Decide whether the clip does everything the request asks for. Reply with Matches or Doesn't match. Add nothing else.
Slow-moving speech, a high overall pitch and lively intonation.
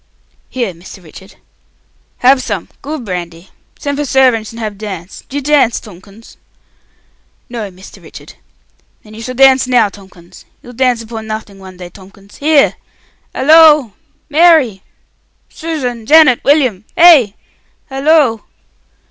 Matches